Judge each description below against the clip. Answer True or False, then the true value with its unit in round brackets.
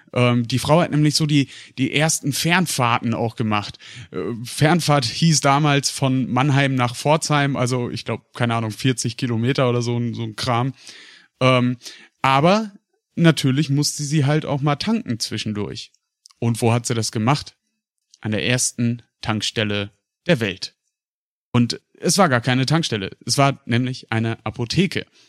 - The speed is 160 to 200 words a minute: False (145 wpm)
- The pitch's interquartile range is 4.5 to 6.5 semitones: False (3.8 semitones)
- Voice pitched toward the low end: True (125 Hz)